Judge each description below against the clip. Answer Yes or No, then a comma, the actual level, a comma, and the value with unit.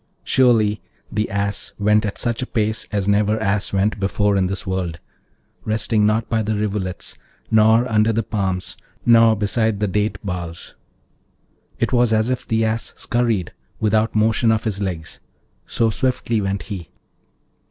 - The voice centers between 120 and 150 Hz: No, low, 105 Hz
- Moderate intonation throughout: No, narrow, 2.0 semitones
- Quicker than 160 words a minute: No, average, 155 wpm